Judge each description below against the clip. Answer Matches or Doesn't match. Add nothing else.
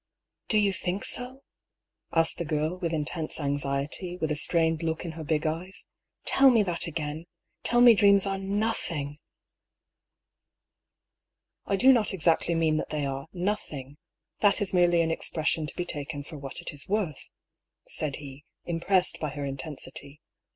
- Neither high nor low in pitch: Matches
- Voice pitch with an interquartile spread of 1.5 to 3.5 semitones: Doesn't match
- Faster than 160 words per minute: Matches